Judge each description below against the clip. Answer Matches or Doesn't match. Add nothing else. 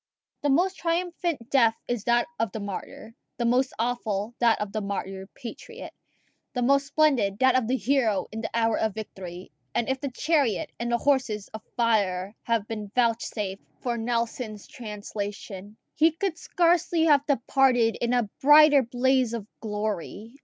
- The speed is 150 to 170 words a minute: Matches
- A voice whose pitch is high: Matches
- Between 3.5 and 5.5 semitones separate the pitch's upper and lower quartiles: Matches